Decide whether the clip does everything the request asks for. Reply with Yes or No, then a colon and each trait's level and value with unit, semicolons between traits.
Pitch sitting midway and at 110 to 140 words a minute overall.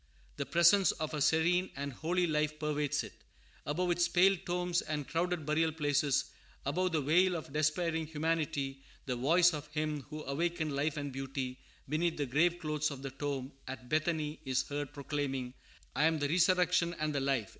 No: medium, 150 Hz; average, 175 wpm